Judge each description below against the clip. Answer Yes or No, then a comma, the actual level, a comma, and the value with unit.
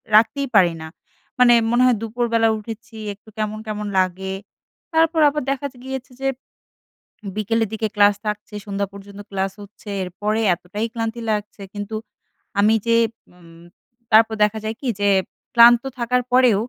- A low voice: No, high, 220 Hz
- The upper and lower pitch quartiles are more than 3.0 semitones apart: No, narrow, 2.6 semitones